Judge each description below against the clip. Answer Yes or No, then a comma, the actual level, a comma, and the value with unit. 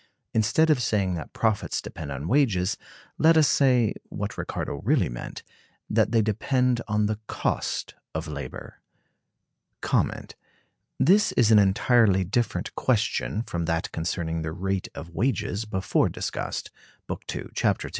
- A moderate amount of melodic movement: No, wide, 6.1 semitones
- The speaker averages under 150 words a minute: Yes, average, 140 wpm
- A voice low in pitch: Yes, low, 105 Hz